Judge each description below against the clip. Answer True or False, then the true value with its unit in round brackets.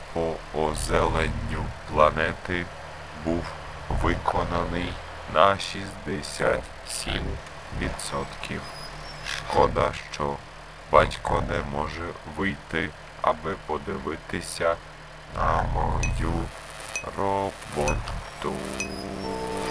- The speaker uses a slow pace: True (55 wpm)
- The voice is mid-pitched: False (80 Hz)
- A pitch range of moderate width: False (2.3 semitones)